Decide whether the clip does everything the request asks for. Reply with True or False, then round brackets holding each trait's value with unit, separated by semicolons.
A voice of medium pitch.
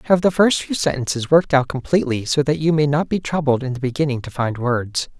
True (145 Hz)